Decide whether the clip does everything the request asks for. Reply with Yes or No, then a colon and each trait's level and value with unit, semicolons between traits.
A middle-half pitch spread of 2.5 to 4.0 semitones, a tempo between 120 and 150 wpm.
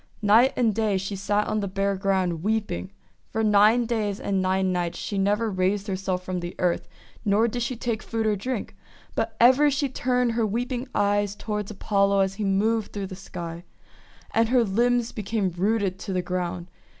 No: average, 3.1 semitones; average, 190 wpm